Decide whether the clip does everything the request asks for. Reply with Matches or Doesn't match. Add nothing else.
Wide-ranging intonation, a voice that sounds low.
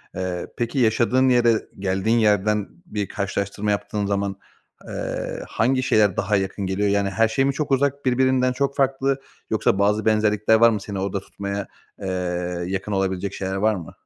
Doesn't match